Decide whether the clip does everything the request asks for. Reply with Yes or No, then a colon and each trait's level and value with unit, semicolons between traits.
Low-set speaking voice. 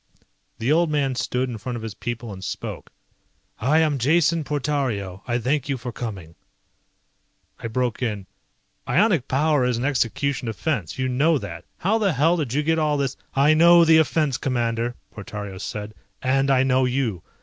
Yes: low, 130 Hz